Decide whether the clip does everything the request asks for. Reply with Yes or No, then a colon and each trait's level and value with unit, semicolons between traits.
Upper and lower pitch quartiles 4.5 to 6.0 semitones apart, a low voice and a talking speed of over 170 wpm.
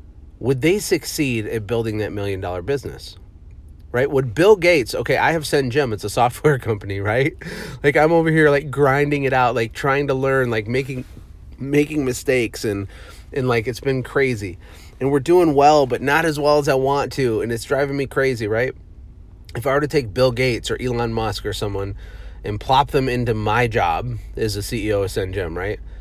Yes: wide, 5.4 semitones; low, 125 Hz; average, 195 wpm